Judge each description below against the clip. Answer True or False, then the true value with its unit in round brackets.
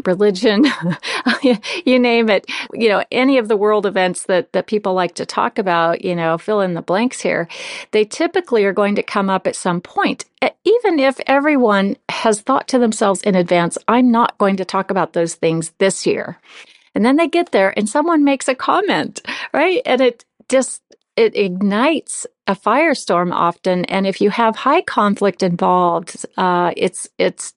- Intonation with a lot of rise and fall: True (6.0 semitones)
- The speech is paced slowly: False (180 wpm)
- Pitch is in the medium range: False (210 Hz)